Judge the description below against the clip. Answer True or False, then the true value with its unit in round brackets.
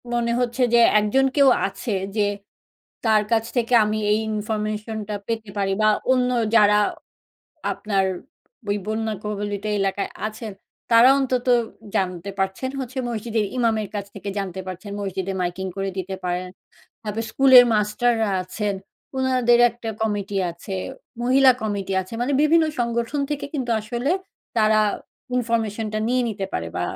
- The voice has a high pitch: True (215 Hz)